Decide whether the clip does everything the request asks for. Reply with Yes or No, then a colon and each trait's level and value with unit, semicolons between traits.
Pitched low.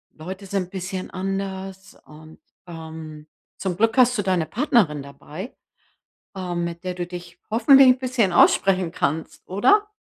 No: medium, 185 Hz